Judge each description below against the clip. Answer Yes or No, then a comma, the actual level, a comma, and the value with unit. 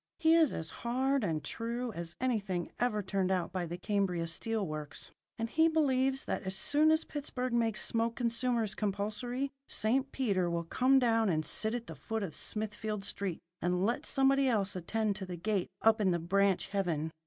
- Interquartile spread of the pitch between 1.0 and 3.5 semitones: No, average, 5.0 semitones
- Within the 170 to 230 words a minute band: Yes, average, 190 wpm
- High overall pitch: Yes, high, 215 Hz